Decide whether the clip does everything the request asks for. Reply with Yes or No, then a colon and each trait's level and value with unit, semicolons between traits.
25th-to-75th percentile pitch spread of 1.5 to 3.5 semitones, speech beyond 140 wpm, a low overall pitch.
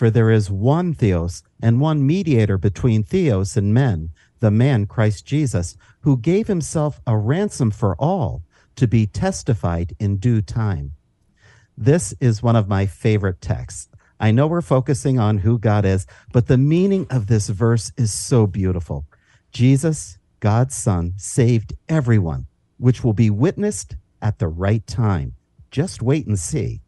No: average, 4.6 semitones; average, 155 wpm; low, 110 Hz